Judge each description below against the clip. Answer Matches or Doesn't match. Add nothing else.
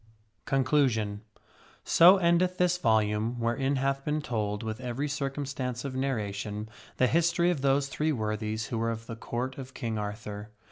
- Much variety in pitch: Doesn't match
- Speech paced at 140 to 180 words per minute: Matches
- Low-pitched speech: Matches